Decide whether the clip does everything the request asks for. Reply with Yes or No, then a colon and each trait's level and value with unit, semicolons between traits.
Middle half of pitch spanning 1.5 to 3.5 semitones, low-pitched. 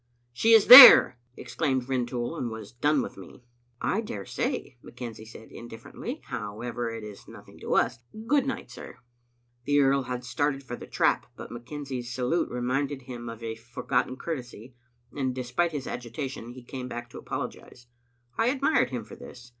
Yes: average, 3.0 semitones; low, 125 Hz